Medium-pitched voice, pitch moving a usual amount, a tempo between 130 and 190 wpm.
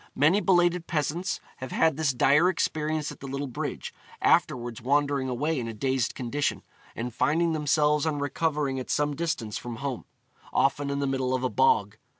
Yes: medium, 145 Hz; average, 3.2 semitones; average, 175 wpm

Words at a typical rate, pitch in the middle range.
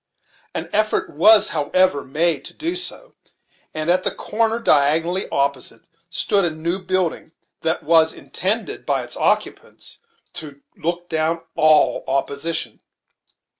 No: slow, 130 wpm; medium, 165 Hz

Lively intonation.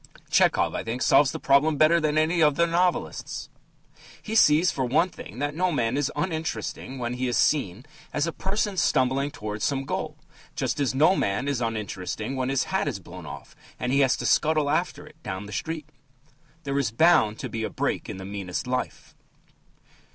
No: average, 4.6 semitones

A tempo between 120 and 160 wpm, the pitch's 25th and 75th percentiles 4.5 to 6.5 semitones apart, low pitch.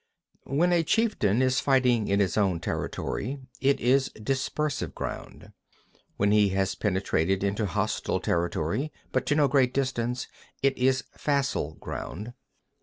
Yes: average, 145 wpm; wide, 5.5 semitones; low, 125 Hz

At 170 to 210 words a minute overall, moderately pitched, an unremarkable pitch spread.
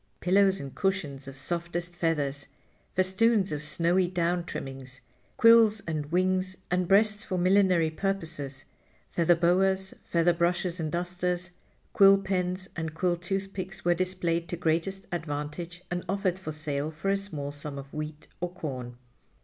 No: average, 145 wpm; medium, 175 Hz; average, 3.2 semitones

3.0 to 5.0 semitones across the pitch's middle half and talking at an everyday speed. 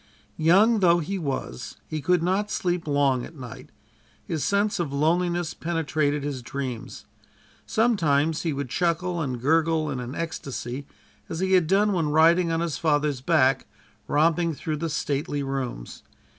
Yes: average, 3.7 semitones; average, 155 wpm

